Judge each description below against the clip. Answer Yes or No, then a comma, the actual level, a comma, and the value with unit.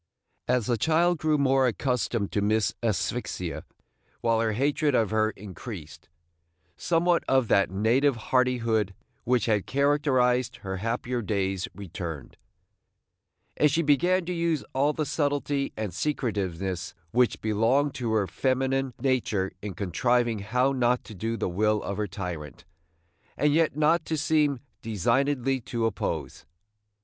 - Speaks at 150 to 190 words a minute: No, average, 140 wpm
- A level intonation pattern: No, average, 5.1 semitones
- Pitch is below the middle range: Yes, low, 120 Hz